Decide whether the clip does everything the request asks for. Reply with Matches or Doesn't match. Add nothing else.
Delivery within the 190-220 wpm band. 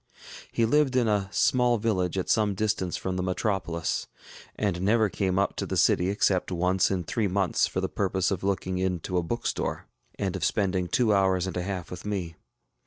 Matches